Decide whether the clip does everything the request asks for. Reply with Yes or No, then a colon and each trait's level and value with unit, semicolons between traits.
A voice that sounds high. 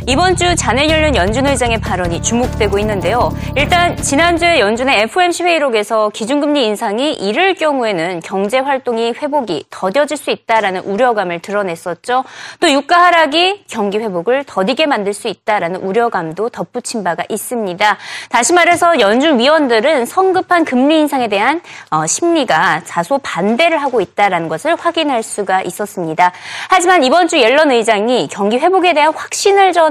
Yes: high, 245 Hz